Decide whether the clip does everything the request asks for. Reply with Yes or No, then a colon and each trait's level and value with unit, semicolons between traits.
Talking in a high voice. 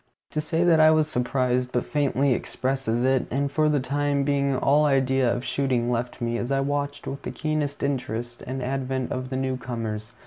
No: low, 135 Hz